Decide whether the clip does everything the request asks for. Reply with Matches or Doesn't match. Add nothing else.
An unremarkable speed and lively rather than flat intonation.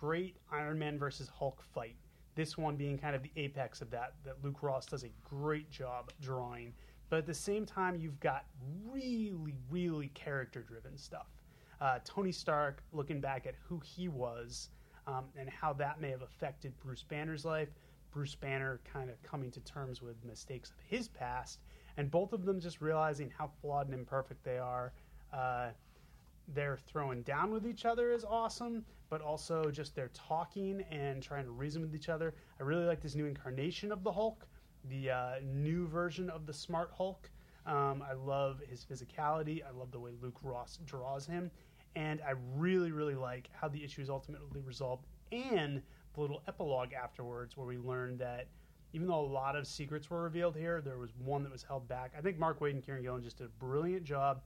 Doesn't match